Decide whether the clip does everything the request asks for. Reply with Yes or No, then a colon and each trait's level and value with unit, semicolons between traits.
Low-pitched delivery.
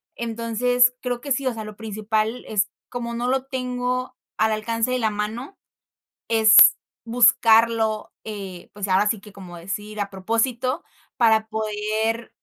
No: high, 225 Hz